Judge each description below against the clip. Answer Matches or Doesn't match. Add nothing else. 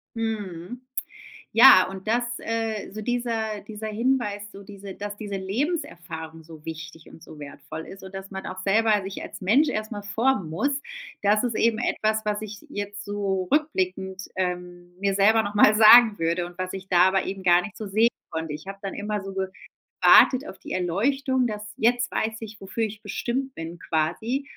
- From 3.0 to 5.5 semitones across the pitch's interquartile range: Matches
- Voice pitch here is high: Matches